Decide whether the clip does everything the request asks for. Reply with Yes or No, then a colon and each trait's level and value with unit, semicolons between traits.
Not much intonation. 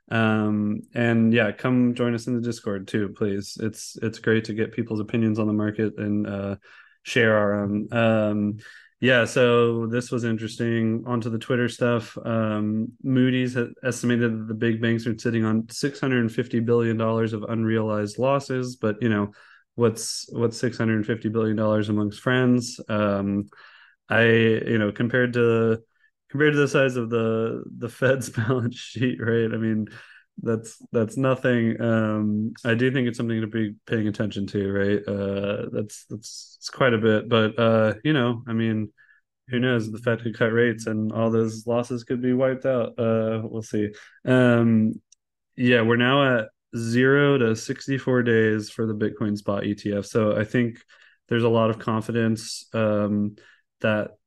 Yes: narrow, 1.9 semitones